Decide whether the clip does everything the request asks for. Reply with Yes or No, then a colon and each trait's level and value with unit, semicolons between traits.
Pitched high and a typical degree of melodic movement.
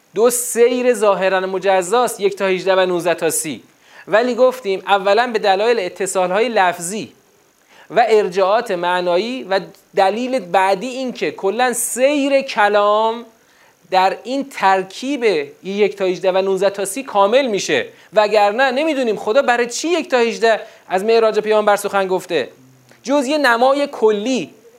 Yes: high, 215 Hz; average, 4.5 semitones